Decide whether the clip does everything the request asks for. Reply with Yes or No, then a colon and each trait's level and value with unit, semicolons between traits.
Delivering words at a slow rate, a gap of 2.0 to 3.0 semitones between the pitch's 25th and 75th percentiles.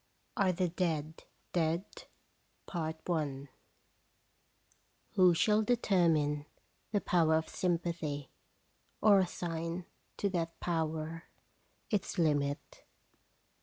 Yes: slow, 95 wpm; narrow, 2.5 semitones